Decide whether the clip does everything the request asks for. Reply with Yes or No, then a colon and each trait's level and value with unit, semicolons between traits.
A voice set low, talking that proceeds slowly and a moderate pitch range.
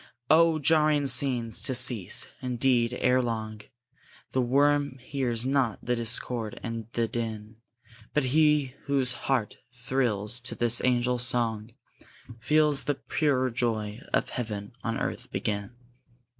Yes: low, 125 Hz; slow, 130 wpm; average, 3.0 semitones